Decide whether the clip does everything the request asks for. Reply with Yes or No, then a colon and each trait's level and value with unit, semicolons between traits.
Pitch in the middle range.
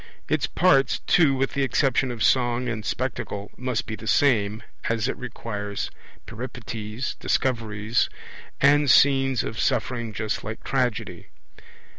No: low, 120 Hz